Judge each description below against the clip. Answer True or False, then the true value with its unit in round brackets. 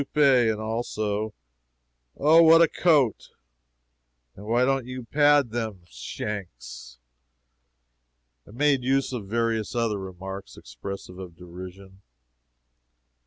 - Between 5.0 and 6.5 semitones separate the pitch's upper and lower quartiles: True (5.3 semitones)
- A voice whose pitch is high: False (110 Hz)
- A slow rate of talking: True (105 wpm)